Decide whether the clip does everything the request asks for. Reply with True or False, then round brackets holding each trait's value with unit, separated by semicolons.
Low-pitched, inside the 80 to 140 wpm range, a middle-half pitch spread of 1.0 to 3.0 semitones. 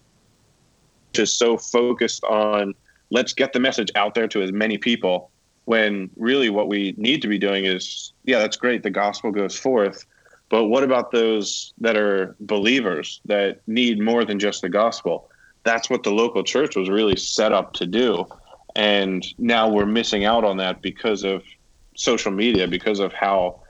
False (105 Hz; 175 wpm; 2.7 semitones)